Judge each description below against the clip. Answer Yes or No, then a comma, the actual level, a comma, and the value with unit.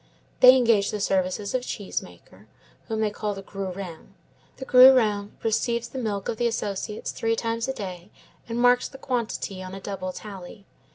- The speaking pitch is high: Yes, high, 210 Hz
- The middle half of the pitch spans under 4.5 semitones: Yes, average, 3.3 semitones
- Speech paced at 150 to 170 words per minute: No, average, 180 wpm